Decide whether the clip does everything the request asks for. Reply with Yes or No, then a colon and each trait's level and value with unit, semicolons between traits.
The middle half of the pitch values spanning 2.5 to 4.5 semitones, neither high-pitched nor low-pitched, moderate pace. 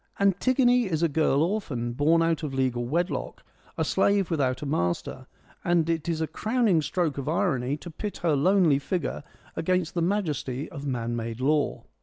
No: average, 4.9 semitones; medium, 160 Hz; average, 180 wpm